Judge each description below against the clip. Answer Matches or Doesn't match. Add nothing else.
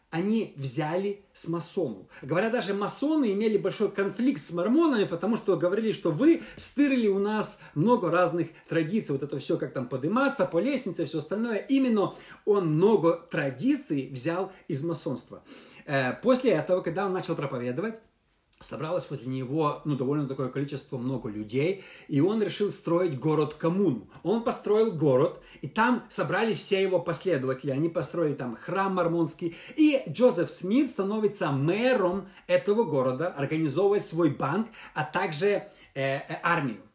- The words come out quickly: Doesn't match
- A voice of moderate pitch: Matches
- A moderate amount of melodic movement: Matches